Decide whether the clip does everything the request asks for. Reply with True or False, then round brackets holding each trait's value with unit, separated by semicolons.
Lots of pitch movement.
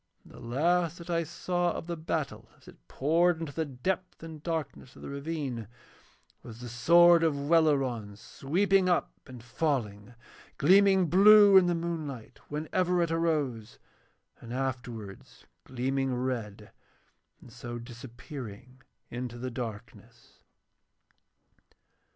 True (5.8 semitones)